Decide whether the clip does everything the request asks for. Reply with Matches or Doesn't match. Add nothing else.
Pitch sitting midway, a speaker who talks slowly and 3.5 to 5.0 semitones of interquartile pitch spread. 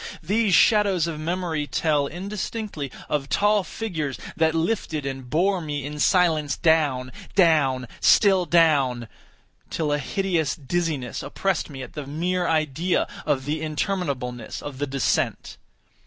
Matches